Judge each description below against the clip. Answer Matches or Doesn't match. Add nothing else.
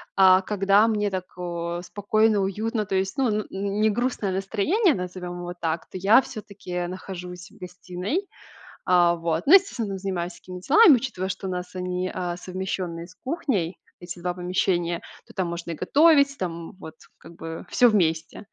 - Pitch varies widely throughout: Doesn't match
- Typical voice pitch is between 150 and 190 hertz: Matches